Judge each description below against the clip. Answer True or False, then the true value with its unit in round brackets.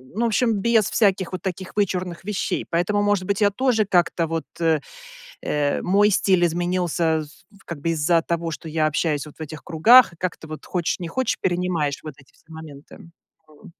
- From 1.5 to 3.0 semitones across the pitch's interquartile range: False (3.8 semitones)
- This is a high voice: False (175 Hz)